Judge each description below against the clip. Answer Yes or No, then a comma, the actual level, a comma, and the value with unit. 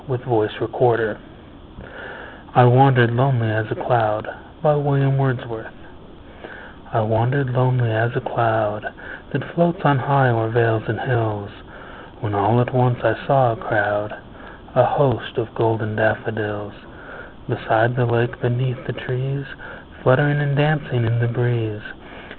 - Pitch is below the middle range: Yes, low, 120 Hz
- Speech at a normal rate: No, slow, 125 wpm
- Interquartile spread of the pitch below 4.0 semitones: Yes, average, 2.7 semitones